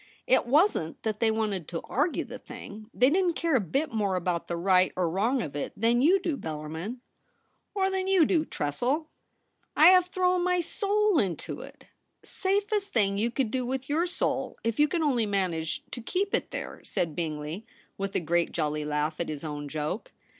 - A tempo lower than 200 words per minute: No, fast, 205 wpm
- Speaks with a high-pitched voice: Yes, high, 225 Hz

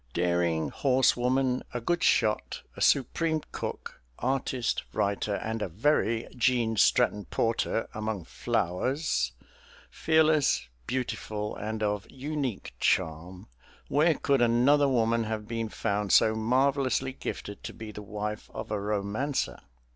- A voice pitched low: Yes, low, 115 Hz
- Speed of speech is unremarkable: No, slow, 125 wpm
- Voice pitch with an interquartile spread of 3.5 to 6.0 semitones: Yes, average, 4.2 semitones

